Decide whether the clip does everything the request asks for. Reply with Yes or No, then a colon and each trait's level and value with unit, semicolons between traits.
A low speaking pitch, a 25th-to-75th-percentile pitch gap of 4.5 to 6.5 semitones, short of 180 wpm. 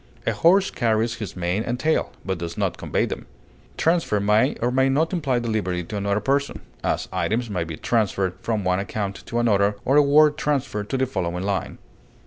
No: low, 110 Hz; average, 5.3 semitones; average, 195 wpm